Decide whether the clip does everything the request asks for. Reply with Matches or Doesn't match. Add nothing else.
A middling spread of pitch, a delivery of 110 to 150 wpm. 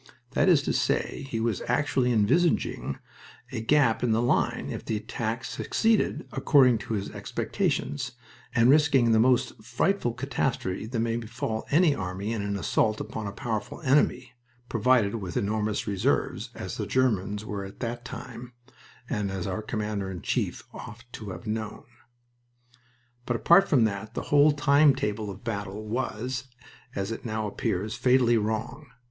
Doesn't match